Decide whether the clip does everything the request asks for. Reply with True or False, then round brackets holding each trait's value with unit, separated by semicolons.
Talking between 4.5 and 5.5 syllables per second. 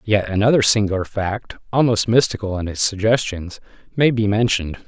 True (5.4 syllables/s)